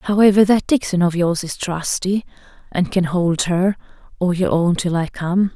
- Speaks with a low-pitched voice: No, medium, 185 Hz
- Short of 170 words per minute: No, average, 185 wpm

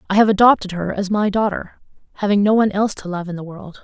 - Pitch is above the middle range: Yes, high, 200 Hz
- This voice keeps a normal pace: No, fast, 250 wpm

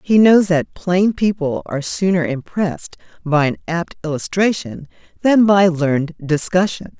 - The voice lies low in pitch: No, medium, 175 Hz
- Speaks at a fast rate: No, slow, 135 wpm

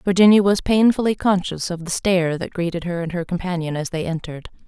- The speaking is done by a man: No, female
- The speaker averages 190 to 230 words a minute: Yes, fast, 205 wpm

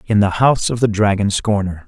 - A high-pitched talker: No, low, 105 Hz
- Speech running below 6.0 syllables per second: Yes, 5.8 syllables/s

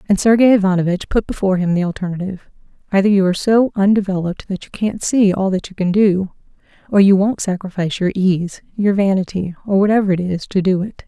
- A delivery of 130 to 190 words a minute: No, average, 200 wpm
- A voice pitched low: No, high, 195 Hz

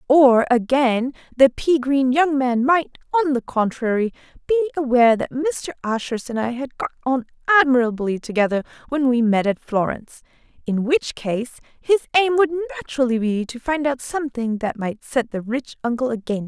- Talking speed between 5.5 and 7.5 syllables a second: No, 5.2 syllables/s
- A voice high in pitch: Yes, very high, 260 Hz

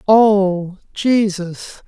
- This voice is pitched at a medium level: No, high, 195 Hz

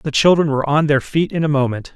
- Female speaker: No, male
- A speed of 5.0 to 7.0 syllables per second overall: Yes, 6.3 syllables/s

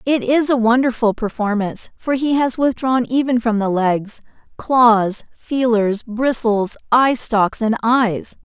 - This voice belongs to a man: No, female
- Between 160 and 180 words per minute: No, average, 140 wpm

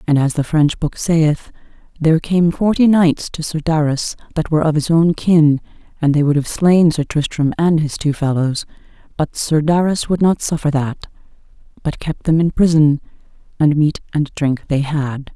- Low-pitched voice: No, medium, 155 Hz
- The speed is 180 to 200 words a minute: Yes, average, 190 wpm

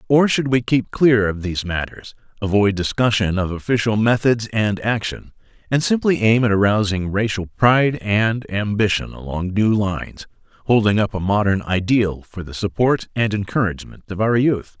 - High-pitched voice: No, low, 105 Hz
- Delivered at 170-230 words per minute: No, average, 160 wpm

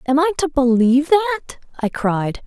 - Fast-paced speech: No, average, 170 wpm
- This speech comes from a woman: Yes, female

